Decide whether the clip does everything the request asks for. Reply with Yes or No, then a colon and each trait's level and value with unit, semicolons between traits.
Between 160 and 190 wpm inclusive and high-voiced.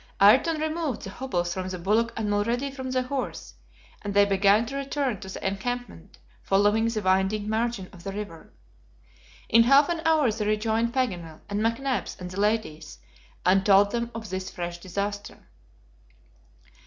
Yes: average, 165 wpm; high, 210 Hz